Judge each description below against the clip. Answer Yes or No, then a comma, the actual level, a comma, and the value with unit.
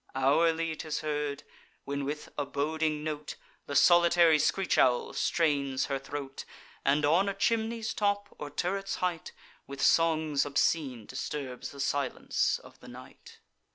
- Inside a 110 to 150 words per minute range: Yes, average, 140 wpm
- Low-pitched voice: No, medium, 150 Hz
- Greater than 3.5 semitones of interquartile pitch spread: No, average, 3.2 semitones